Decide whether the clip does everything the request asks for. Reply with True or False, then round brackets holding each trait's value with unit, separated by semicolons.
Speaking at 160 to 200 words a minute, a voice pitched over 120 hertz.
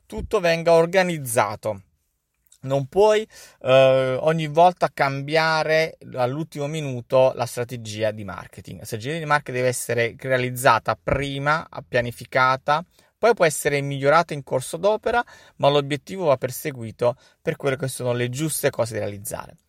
False (135 wpm; 140 Hz)